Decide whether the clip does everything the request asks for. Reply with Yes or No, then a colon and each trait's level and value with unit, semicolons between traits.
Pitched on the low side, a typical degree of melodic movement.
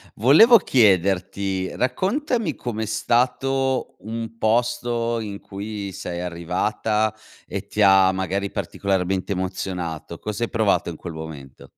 Yes: low, 100 Hz; average, 4.0 semitones